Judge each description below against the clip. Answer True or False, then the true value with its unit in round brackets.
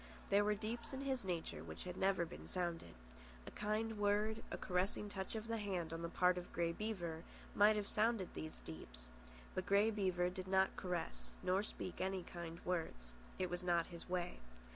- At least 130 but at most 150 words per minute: False (185 wpm)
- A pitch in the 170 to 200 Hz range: True (185 Hz)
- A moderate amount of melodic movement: True (3.2 semitones)